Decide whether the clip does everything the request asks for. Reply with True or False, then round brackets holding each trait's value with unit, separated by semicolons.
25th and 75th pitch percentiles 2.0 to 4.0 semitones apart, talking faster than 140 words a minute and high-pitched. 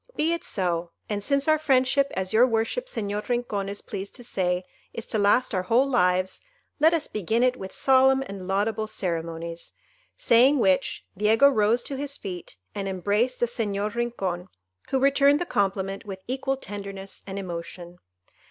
False (5.1 semitones; 165 wpm; 210 Hz)